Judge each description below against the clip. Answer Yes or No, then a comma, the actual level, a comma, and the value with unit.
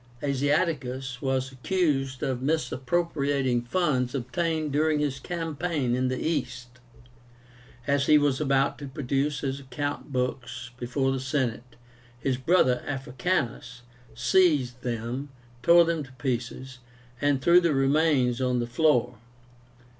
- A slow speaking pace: Yes, slow, 125 wpm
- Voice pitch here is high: No, low, 135 Hz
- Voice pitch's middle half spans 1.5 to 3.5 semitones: Yes, average, 2.9 semitones